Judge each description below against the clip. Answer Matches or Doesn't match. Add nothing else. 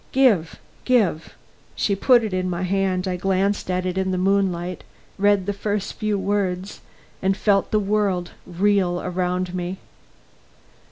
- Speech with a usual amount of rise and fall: Doesn't match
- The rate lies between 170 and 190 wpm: Doesn't match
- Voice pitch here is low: Doesn't match